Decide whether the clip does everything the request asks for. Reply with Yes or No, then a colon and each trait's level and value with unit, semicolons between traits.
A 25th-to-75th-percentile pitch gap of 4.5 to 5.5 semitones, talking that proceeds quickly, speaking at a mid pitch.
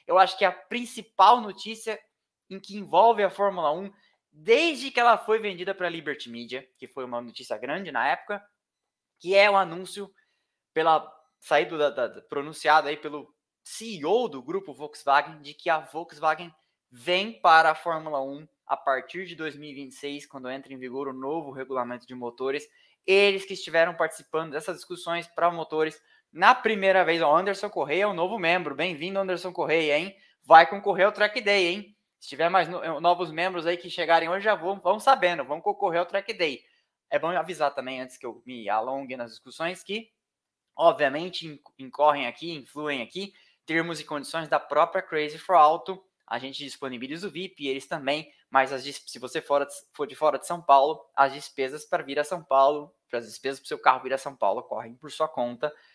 Yes: average, 5.1 semitones; fast, 190 wpm; medium, 160 Hz